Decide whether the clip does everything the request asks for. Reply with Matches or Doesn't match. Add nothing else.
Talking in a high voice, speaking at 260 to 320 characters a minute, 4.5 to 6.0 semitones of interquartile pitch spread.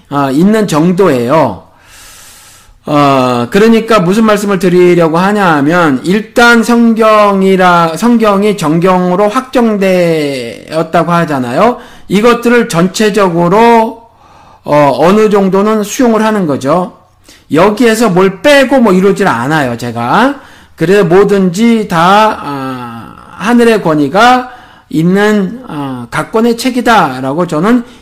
Doesn't match